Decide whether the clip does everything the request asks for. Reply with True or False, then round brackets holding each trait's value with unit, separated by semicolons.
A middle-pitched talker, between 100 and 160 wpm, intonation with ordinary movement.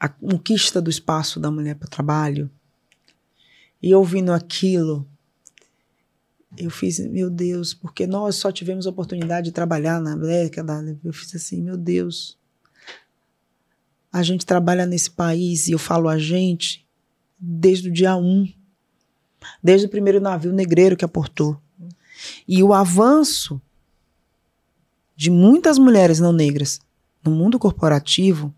True (175 Hz; 135 wpm; 3.3 semitones)